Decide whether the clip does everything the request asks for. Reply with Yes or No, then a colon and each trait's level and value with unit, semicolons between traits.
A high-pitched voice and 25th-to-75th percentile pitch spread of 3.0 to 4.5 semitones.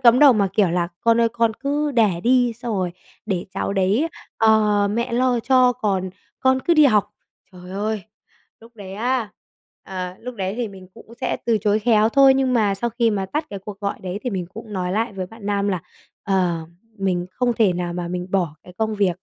Yes: high, 210 Hz; average, 4.0 semitones